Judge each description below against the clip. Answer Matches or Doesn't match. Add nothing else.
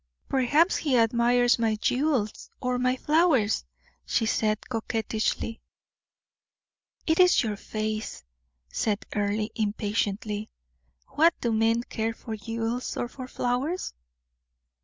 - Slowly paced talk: Matches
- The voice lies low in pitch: Doesn't match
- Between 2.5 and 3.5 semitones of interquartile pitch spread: Matches